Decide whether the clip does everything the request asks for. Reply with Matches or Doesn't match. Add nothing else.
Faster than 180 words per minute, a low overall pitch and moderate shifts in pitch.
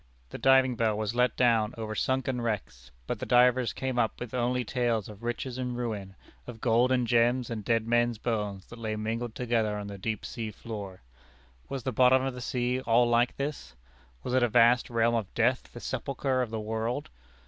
Doesn't match